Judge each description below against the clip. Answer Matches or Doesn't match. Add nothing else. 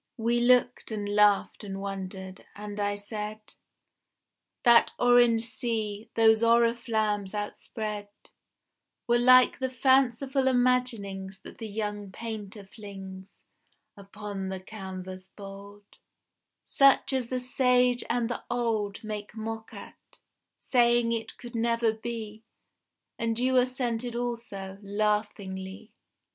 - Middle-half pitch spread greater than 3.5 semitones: Doesn't match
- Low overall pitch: Doesn't match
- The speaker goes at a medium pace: Doesn't match